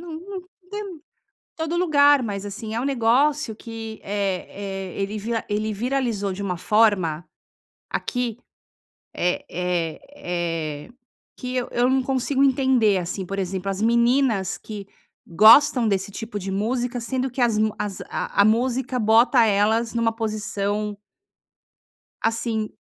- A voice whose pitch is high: Yes, high, 220 Hz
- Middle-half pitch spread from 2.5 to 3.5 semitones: No, average, 4.1 semitones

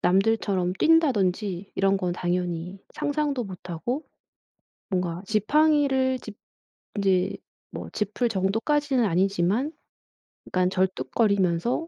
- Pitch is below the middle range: No, high, 200 Hz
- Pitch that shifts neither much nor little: No, wide, 5.9 semitones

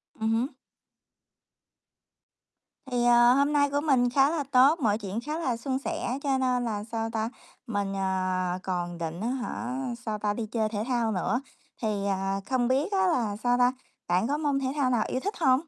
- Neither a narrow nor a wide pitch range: Yes, average, 4.3 semitones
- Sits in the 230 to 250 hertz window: Yes, high, 240 Hz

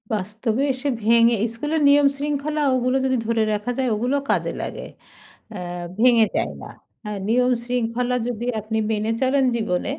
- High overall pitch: Yes, high, 240 Hz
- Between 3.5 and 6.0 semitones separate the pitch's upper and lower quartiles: No, average, 3.0 semitones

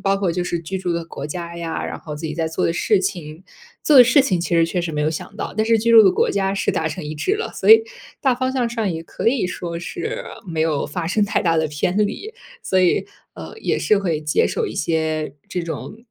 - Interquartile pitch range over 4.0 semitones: Yes, average, 4.7 semitones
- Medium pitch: Yes, medium, 175 Hz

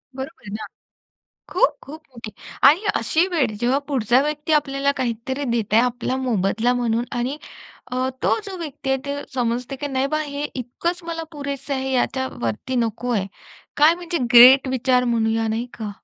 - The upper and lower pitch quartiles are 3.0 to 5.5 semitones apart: Yes, average, 3.5 semitones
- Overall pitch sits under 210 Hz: No, very high, 260 Hz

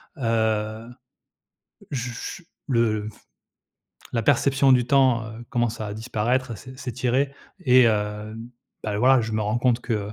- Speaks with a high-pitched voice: No, low, 115 Hz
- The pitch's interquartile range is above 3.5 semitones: No, average, 2.8 semitones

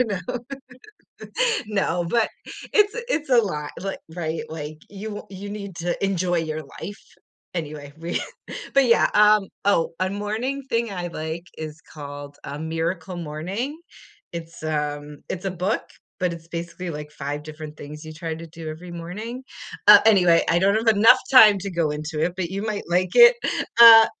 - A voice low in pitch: No, medium, 175 Hz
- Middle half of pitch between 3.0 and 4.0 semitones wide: No, average, 4.7 semitones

